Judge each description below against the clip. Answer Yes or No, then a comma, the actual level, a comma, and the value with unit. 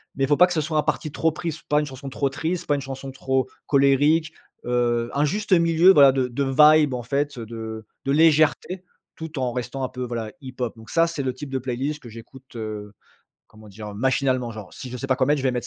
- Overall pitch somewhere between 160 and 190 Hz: No, low, 135 Hz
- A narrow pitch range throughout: No, average, 3.5 semitones